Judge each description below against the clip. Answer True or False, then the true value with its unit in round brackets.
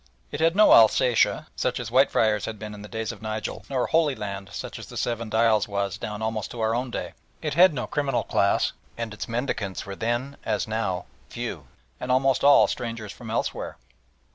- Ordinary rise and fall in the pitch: True (3.0 semitones)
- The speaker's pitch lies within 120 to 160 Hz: False (110 Hz)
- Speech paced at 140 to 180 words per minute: False (200 wpm)